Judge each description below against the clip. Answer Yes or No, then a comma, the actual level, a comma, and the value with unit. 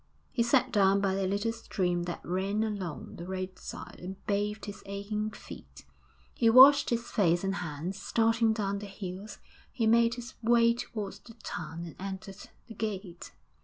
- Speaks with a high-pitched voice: Yes, high, 200 Hz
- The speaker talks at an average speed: Yes, average, 165 wpm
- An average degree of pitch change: Yes, average, 3.3 semitones